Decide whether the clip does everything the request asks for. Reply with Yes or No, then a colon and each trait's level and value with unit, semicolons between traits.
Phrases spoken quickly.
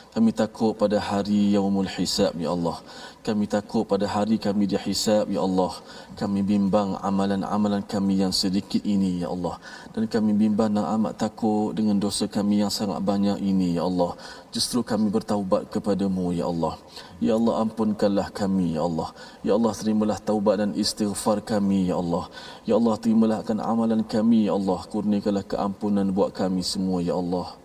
Yes: fast, 165 wpm